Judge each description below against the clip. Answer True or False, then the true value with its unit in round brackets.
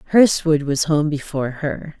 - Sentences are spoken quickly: False (150 wpm)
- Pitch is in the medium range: True (150 Hz)